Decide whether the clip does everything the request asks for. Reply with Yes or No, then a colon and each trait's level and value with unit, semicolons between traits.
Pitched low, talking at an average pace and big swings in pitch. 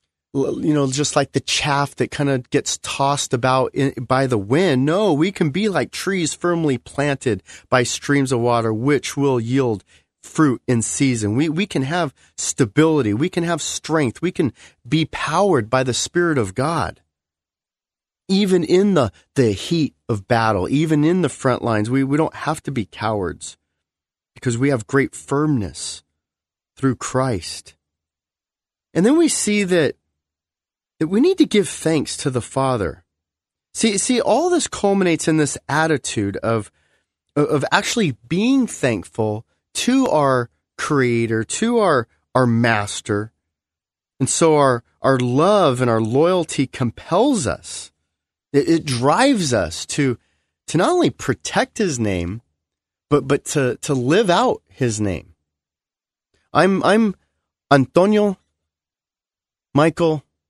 Yes: low, 130 Hz; average, 145 wpm; wide, 8.2 semitones